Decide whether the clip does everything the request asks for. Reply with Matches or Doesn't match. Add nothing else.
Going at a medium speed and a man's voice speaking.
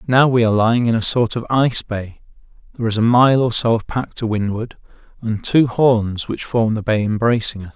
Doesn't match